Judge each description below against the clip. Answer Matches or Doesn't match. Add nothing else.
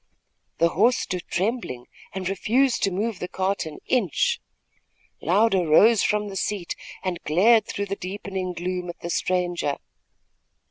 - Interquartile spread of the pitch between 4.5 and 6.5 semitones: Doesn't match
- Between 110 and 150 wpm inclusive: Matches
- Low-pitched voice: Doesn't match